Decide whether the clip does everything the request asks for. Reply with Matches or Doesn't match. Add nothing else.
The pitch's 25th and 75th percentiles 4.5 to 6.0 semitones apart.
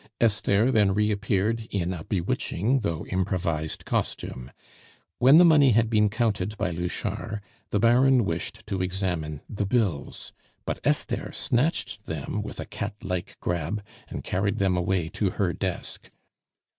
Doesn't match